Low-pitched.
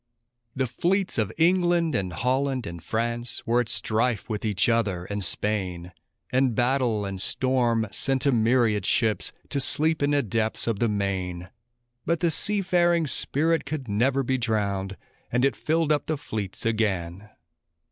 Yes: low, 120 Hz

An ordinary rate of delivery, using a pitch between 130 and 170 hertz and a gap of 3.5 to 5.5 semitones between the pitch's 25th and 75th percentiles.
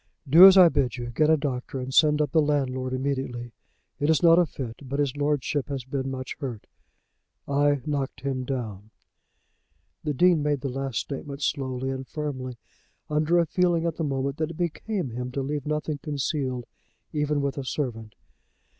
No: average, 180 wpm; medium, 140 Hz; average, 2.7 semitones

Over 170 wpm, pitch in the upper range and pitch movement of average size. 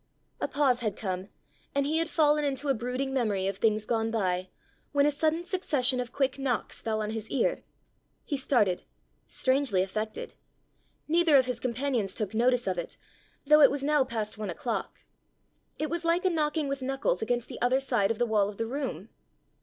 Yes: average, 195 wpm; very high, 250 Hz; average, 4.7 semitones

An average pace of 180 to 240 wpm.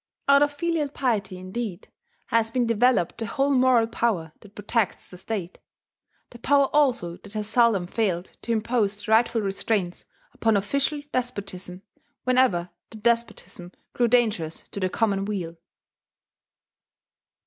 No: slow, 135 wpm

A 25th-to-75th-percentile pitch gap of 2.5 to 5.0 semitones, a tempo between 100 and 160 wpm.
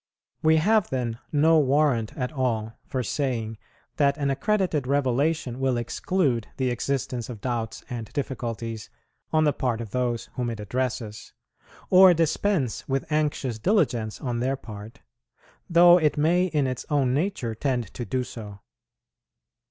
Yes: average, 4.5 semitones; average, 145 wpm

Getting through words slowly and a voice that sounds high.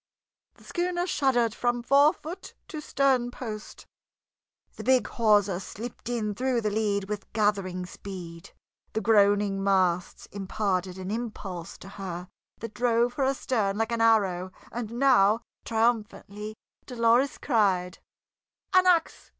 Yes: slow, 125 wpm; high, 220 Hz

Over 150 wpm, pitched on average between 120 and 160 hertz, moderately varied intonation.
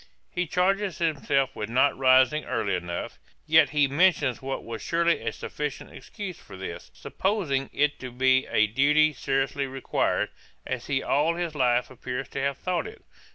Yes: average, 165 wpm; medium, 140 Hz; average, 3.7 semitones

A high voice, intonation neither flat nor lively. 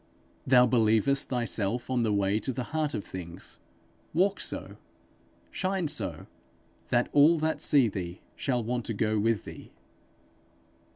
No: low, 120 Hz; average, 4.7 semitones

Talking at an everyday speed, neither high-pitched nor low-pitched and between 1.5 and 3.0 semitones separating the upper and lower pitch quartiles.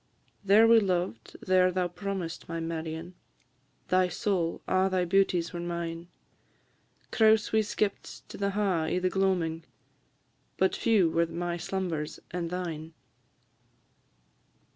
No: slow, 125 wpm; medium, 180 Hz; narrow, 2.5 semitones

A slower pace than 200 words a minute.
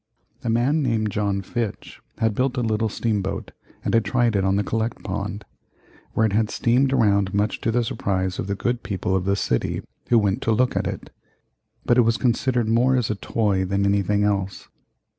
No: fast, 205 wpm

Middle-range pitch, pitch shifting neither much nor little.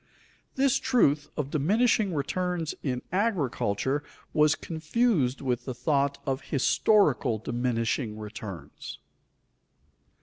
No: medium, 145 Hz; wide, 6.4 semitones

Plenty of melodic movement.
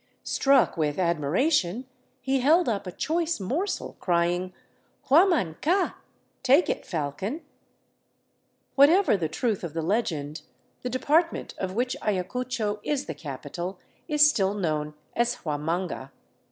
Yes: wide, 8.4 semitones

